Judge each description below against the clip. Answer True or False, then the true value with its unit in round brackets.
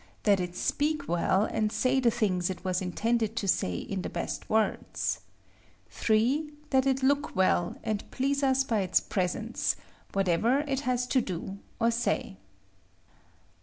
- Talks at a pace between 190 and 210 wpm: False (155 wpm)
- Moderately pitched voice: False (220 Hz)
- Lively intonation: True (5.8 semitones)